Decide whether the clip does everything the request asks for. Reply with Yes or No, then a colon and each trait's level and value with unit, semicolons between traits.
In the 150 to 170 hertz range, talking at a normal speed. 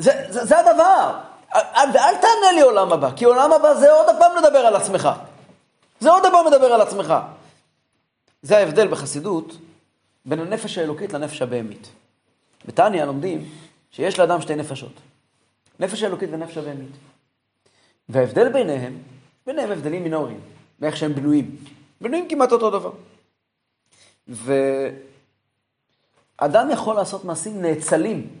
Yes: medium, 165 Hz; average, 125 wpm